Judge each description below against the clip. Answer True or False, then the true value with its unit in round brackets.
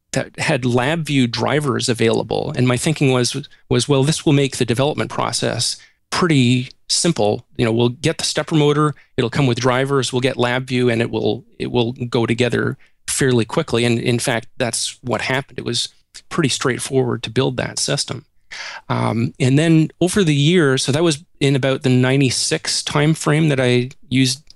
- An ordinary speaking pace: True (180 wpm)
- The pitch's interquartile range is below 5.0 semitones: True (3.5 semitones)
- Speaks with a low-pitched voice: True (130 Hz)